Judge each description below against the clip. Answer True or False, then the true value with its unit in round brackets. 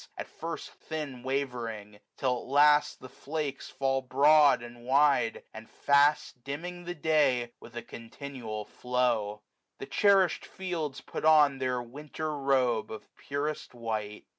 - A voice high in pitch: False (135 Hz)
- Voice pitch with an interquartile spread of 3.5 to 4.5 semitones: True (3.8 semitones)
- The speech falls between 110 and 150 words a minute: True (140 wpm)